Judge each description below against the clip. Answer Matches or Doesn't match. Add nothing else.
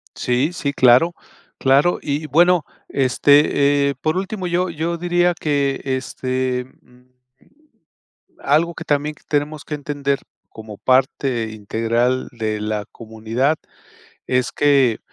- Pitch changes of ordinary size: Matches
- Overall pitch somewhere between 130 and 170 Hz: Matches